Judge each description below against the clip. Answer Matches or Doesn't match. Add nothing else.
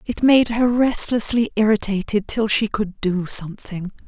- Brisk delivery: Doesn't match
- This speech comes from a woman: Matches